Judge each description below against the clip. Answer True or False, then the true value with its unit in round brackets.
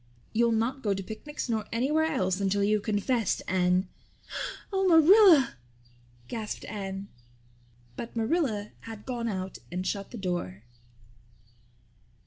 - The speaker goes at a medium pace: False (120 wpm)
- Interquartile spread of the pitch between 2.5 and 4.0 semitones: False (5.2 semitones)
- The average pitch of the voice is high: True (220 Hz)